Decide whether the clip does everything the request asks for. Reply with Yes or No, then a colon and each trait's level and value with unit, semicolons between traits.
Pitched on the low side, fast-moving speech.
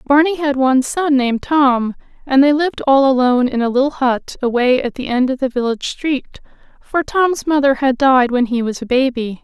No: very high, 265 Hz; fast, 210 wpm